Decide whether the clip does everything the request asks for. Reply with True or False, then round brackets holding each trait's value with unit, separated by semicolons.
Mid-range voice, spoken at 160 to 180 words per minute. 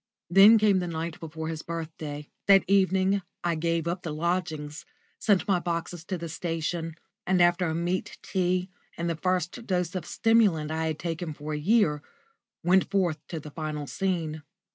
True (170 Hz; 175 wpm)